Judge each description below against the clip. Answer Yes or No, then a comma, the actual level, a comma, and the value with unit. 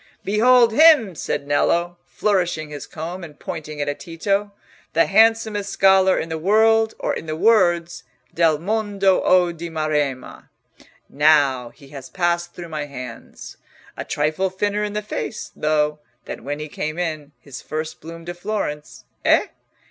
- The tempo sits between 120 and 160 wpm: Yes, average, 155 wpm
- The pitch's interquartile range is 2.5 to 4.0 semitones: No, average, 4.9 semitones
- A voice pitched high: No, medium, 170 Hz